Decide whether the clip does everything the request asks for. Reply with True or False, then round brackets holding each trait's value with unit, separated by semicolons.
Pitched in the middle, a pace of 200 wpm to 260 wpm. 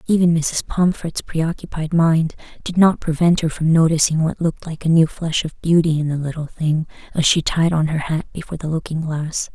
True (160 Hz; 205 wpm)